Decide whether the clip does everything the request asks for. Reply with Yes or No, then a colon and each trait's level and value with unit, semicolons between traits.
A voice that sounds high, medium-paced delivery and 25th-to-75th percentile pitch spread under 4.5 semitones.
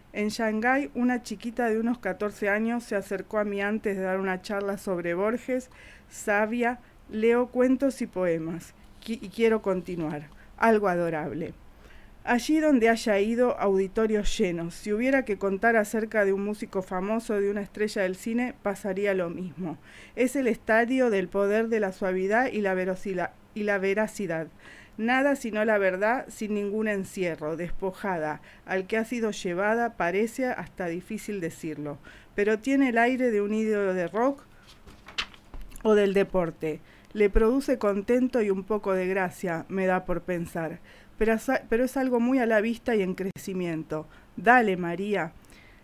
Yes: high, 205 Hz; average, 160 wpm; average, 3.6 semitones